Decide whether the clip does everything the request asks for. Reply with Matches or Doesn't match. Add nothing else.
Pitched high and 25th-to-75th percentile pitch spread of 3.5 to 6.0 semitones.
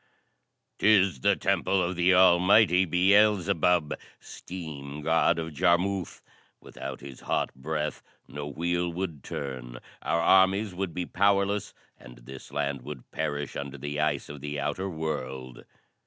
Doesn't match